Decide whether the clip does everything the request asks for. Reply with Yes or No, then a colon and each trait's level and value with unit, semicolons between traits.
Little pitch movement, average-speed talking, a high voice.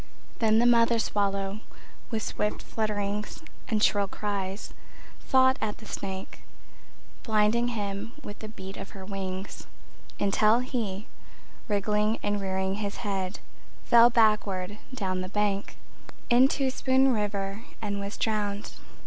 No: narrow, 2.2 semitones; slow, 125 wpm; high, 210 Hz